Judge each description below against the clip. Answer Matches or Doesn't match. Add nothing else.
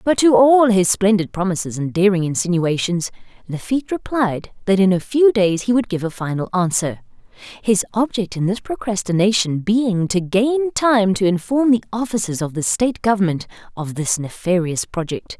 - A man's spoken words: Doesn't match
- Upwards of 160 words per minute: Matches